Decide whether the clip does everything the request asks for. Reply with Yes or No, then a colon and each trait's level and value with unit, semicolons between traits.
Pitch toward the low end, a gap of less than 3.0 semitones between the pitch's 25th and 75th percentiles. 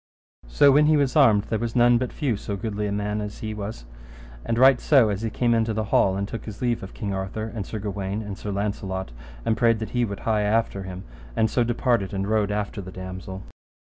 Yes: low, 105 Hz; narrow, 2.6 semitones